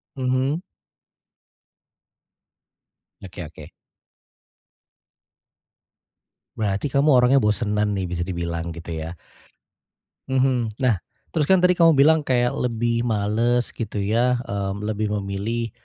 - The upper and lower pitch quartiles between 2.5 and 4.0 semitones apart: No, average, 4.5 semitones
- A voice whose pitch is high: No, low, 115 Hz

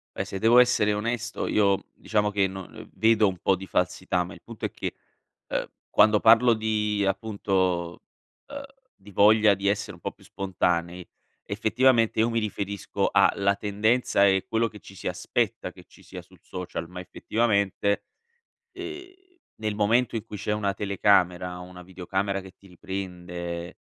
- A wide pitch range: No, average, 2.8 semitones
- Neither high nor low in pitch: No, low, 100 Hz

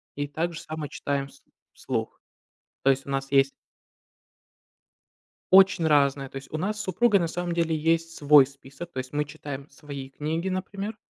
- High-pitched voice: No, medium, 150 Hz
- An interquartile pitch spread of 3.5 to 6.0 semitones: Yes, average, 3.8 semitones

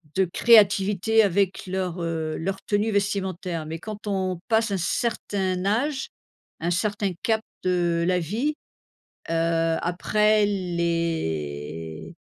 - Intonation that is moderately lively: Yes, average, 3.6 semitones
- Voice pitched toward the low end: No, high, 190 Hz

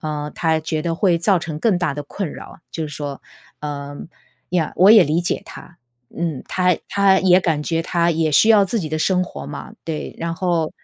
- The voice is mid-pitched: Yes, medium, 165 Hz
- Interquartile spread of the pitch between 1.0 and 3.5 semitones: Yes, average, 2.9 semitones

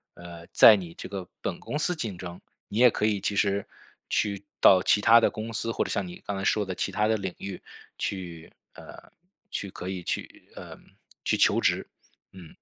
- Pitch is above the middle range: No, low, 100 Hz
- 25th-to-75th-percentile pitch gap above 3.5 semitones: No, average, 2.8 semitones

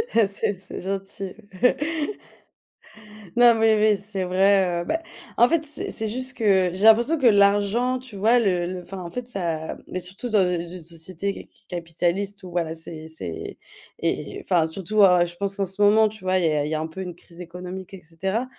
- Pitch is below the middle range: No, high, 190 Hz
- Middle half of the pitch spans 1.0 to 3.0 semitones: No, average, 3.5 semitones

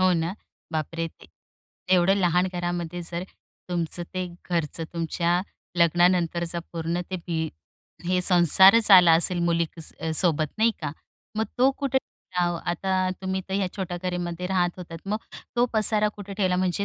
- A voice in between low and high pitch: Yes, medium, 175 Hz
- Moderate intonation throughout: No, narrow, 1.8 semitones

